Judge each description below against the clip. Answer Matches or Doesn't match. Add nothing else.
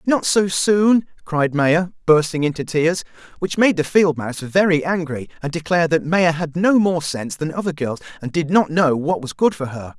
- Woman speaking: Doesn't match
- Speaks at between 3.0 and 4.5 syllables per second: Doesn't match